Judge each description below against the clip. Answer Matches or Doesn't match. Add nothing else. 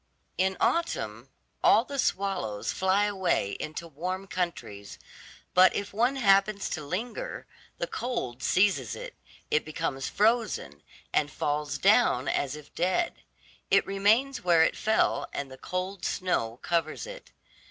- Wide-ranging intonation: Matches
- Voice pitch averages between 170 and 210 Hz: Matches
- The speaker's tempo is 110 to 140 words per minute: Matches